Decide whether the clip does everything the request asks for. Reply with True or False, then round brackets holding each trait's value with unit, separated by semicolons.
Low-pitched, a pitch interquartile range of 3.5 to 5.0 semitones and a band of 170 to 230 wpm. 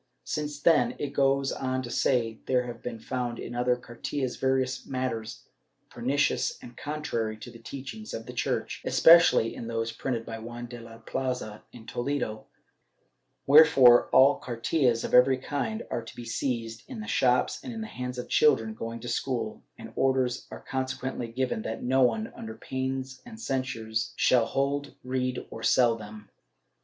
False (125 Hz; 2.6 semitones; 175 wpm)